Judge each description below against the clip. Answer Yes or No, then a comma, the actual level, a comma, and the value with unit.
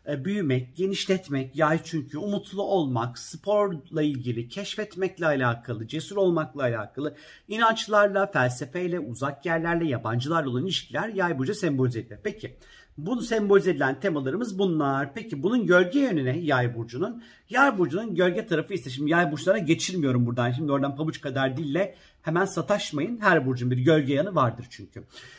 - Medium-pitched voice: Yes, medium, 160 Hz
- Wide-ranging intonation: Yes, wide, 6.2 semitones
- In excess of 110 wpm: Yes, fast, 140 wpm